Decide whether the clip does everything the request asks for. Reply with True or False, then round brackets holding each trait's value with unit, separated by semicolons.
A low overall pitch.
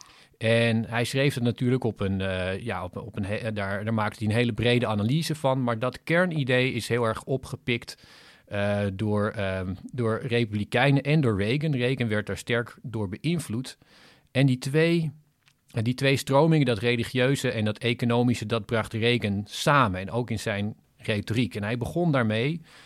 True (120 Hz)